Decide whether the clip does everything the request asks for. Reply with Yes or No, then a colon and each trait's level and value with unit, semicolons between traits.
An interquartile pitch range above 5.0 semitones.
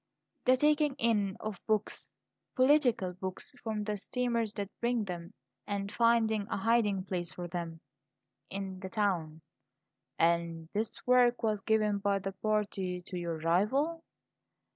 No: average, 4.0 semitones